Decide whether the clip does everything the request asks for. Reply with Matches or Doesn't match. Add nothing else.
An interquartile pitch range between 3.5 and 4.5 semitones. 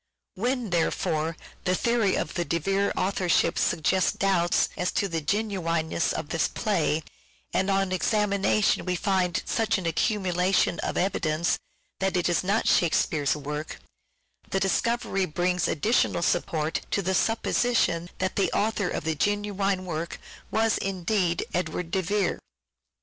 Doesn't match